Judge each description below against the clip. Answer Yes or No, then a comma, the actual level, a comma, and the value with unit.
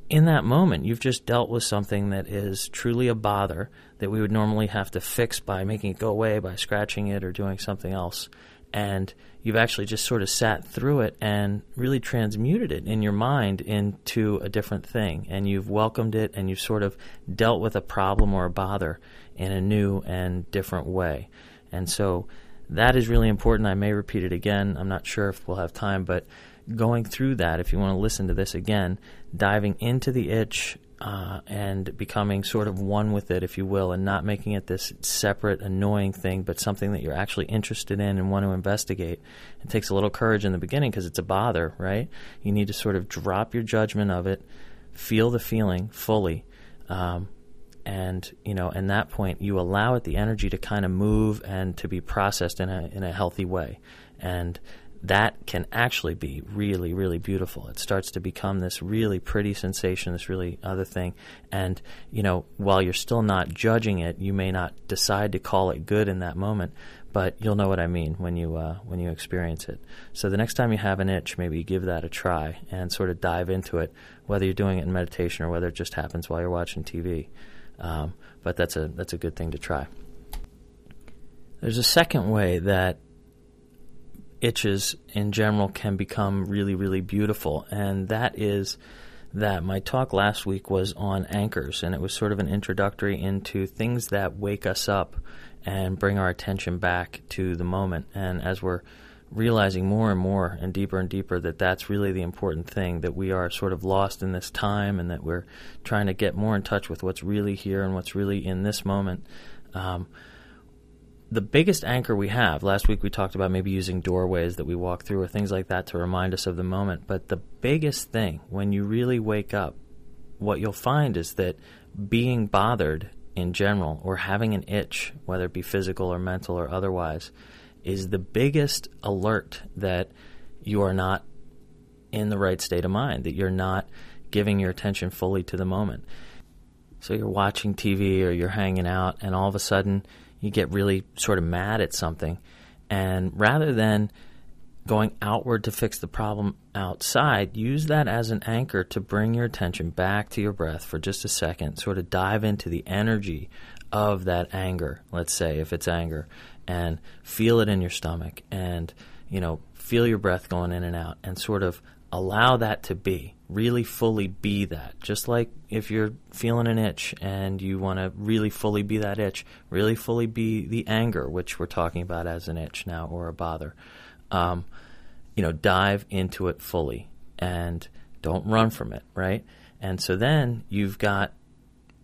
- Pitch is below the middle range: Yes, very low, 95 Hz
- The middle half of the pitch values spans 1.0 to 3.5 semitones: Yes, average, 2.8 semitones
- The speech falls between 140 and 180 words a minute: No, average, 195 wpm